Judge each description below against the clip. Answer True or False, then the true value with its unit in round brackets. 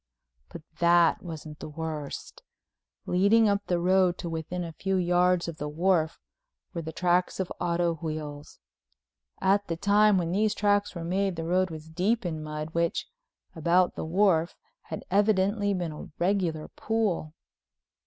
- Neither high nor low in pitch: True (175 Hz)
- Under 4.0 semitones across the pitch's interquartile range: True (3.0 semitones)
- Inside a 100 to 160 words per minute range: True (155 wpm)